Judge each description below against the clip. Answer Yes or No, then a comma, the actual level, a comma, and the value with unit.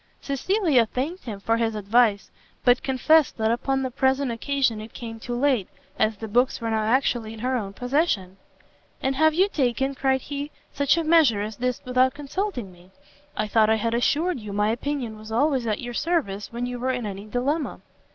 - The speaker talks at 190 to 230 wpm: Yes, average, 200 wpm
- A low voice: No, high, 245 Hz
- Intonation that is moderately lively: Yes, average, 4.0 semitones